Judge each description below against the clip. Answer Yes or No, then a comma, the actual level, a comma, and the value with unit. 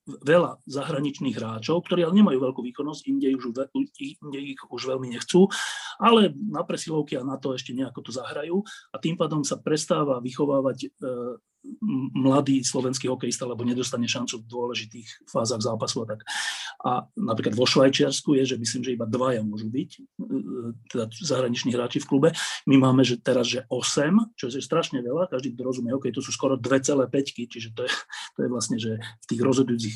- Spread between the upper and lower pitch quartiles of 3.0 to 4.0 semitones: Yes, average, 3.6 semitones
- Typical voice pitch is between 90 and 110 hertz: No, low, 135 Hz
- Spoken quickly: Yes, fast, 180 wpm